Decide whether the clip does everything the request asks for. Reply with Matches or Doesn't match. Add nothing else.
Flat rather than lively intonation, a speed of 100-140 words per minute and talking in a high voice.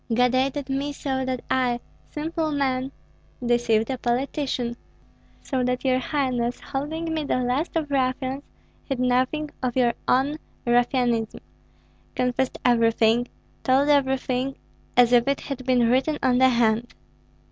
Matches